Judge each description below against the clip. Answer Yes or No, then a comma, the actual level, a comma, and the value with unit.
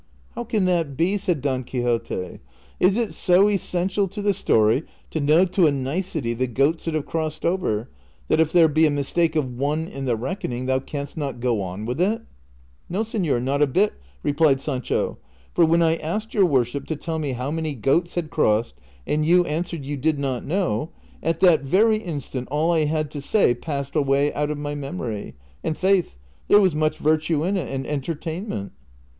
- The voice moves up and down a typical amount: Yes, average, 4.5 semitones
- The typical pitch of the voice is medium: Yes, medium, 150 Hz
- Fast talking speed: Yes, fast, 210 wpm